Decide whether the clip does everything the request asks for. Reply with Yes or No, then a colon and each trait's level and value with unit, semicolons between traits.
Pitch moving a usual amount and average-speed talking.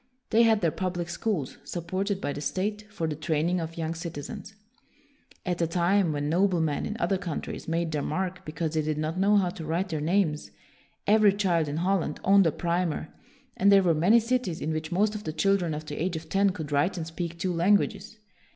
No: average, 3.7 semitones; fast, 215 wpm